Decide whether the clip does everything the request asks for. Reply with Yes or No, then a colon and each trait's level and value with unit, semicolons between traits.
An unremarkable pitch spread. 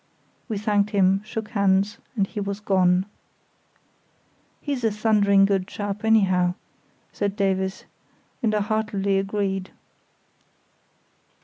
No: narrow, 1.6 semitones